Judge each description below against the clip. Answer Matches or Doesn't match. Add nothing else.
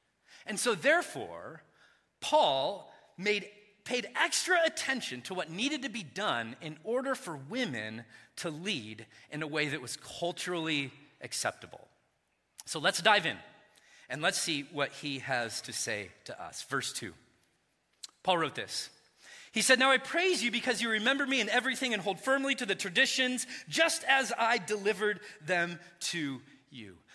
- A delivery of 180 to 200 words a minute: Doesn't match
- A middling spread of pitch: Doesn't match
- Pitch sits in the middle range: Doesn't match